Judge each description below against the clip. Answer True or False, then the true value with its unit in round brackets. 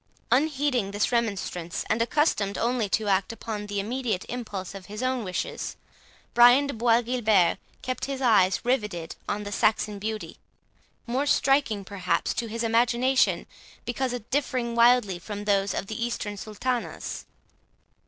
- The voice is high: True (225 Hz)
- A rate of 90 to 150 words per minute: True (145 wpm)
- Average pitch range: True (3.5 semitones)